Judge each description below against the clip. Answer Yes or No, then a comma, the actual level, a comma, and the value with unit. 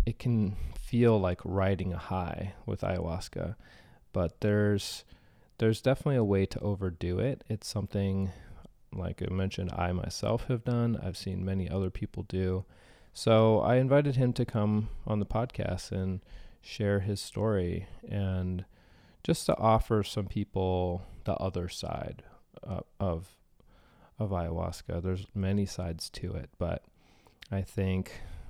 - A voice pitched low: Yes, very low, 95 Hz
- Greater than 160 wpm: No, average, 140 wpm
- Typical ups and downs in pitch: Yes, average, 3.1 semitones